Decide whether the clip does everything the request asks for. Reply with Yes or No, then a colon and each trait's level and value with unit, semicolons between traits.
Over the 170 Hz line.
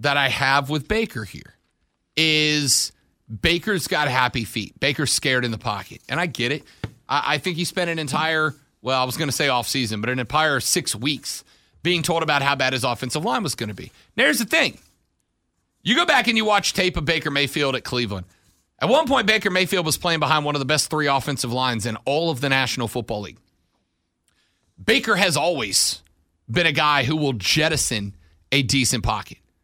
No: medium, 140 Hz